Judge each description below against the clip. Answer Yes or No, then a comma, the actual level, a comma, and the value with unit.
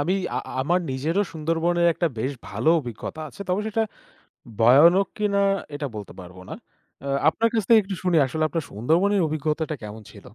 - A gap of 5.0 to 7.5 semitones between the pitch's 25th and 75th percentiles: Yes, wide, 5.6 semitones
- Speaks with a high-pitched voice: No, medium, 160 Hz